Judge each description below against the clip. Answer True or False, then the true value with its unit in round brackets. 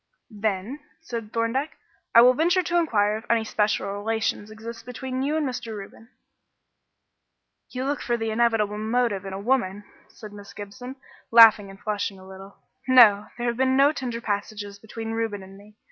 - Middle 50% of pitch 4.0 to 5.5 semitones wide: False (3.3 semitones)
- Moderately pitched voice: False (225 Hz)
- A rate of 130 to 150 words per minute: False (175 wpm)